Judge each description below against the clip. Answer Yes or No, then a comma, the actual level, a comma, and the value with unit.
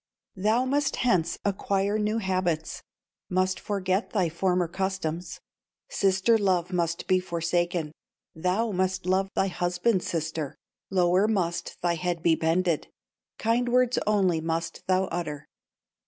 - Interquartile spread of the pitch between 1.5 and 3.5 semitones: Yes, narrow, 2.5 semitones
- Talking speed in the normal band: No, slow, 125 wpm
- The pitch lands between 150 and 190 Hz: Yes, medium, 185 Hz